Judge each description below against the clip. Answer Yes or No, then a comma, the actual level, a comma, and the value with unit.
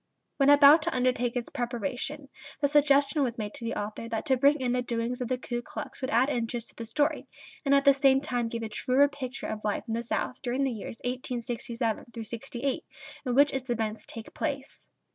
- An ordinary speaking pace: No, fast, 215 wpm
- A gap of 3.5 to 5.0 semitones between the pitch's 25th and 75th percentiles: No, average, 3.0 semitones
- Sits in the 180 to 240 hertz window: No, very high, 250 Hz